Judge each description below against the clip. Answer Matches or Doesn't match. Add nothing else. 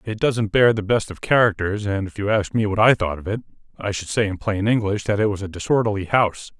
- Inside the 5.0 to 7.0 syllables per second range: Matches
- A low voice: Matches